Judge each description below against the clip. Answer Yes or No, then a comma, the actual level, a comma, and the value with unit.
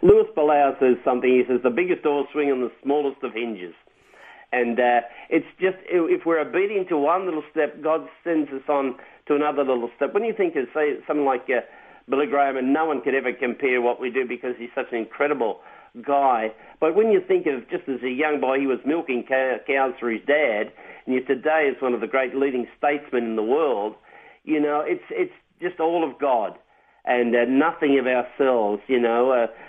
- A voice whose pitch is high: No, low, 135 Hz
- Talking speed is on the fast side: Yes, fast, 215 wpm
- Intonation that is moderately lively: Yes, average, 3.9 semitones